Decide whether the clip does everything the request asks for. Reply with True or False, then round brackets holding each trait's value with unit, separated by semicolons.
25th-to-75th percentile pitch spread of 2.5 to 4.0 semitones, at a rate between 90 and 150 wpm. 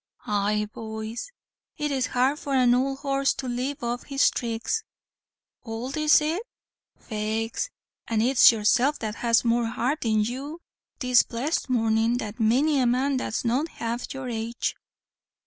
True (3.3 semitones; 145 wpm)